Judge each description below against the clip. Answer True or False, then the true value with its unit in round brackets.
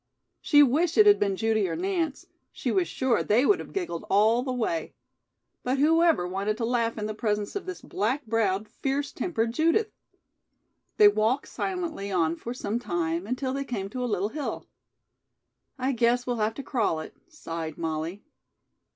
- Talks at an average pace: True (180 wpm)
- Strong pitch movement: True (6.0 semitones)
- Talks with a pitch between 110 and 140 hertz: False (235 Hz)